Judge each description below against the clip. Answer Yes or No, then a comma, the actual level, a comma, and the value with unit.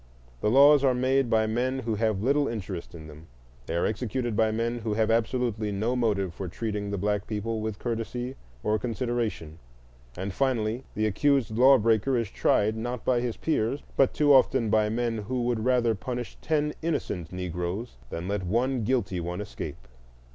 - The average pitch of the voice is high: No, low, 115 Hz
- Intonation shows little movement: No, average, 3.3 semitones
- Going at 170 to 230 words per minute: Yes, average, 180 wpm